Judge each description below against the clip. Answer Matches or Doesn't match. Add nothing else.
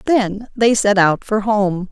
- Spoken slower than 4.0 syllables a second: Matches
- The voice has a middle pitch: Doesn't match